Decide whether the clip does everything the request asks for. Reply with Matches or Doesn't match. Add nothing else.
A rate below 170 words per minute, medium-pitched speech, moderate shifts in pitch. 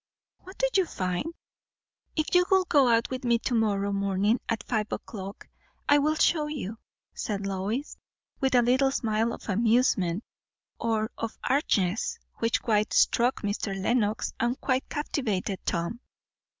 Doesn't match